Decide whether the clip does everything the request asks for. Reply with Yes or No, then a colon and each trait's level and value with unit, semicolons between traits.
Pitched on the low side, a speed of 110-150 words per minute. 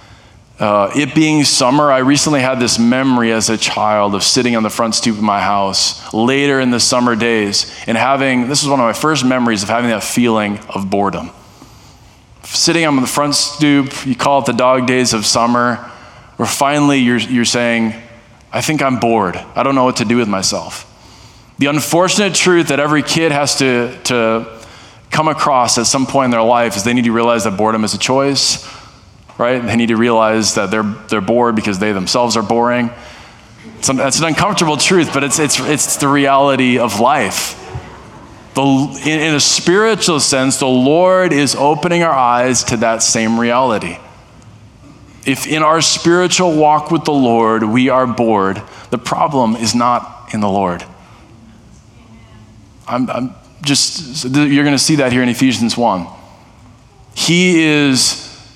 No: low, 120 Hz; average, 175 wpm